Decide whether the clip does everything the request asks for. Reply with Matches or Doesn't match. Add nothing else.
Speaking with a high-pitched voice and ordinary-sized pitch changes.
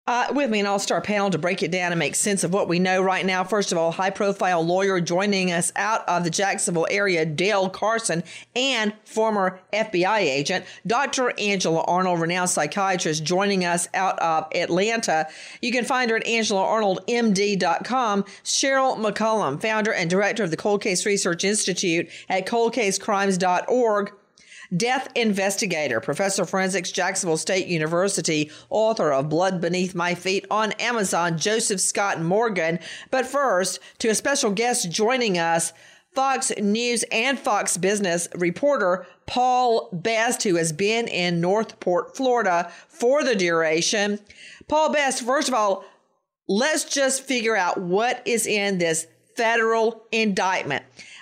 Matches